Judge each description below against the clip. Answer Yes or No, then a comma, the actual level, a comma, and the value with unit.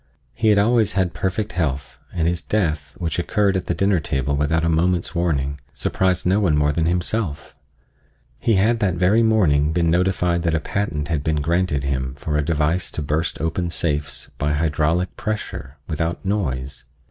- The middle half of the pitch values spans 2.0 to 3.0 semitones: No, average, 3.9 semitones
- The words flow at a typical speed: Yes, average, 180 wpm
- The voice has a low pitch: Yes, very low, 85 Hz